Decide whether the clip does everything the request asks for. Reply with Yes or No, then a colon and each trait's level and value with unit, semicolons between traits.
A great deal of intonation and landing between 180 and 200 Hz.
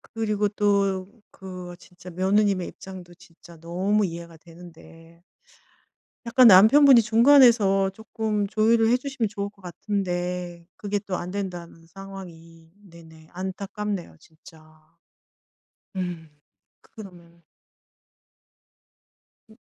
No: average, 3.4 semitones; high, 190 Hz